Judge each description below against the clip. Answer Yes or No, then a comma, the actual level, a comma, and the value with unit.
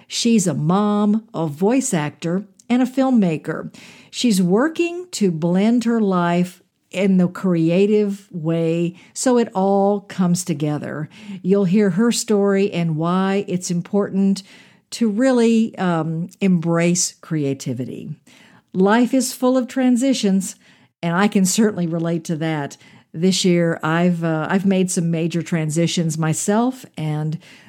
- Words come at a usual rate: No, slow, 130 wpm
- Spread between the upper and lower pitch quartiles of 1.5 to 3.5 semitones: No, average, 3.9 semitones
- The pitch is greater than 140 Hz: Yes, high, 190 Hz